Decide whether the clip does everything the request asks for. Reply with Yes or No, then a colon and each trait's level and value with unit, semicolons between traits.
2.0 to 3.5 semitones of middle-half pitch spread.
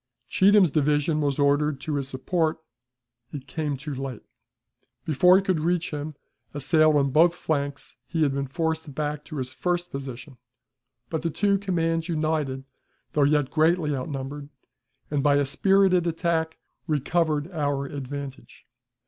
Yes: average, 2.8 semitones